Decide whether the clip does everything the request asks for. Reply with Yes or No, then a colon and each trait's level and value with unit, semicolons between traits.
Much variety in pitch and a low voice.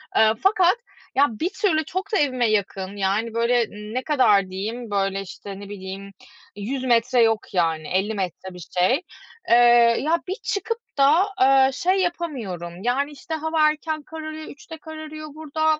No: wide, 7.6 semitones; very high, 255 Hz